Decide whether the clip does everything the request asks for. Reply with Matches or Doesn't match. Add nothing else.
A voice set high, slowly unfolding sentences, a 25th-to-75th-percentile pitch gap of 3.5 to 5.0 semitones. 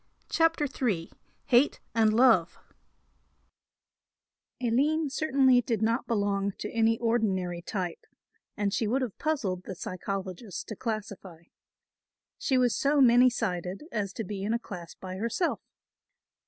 Matches